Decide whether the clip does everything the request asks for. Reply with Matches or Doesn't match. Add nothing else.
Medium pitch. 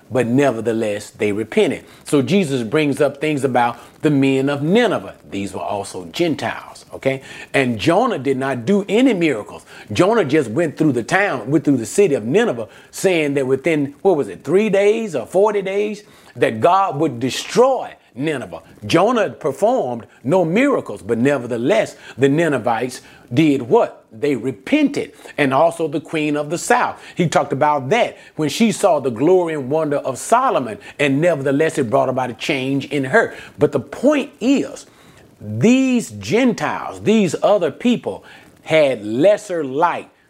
Matches